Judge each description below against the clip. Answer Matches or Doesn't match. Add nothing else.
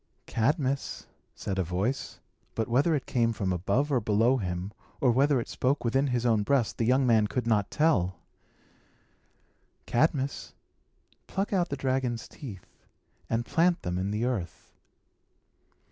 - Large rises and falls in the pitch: Doesn't match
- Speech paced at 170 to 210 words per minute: Doesn't match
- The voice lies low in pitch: Matches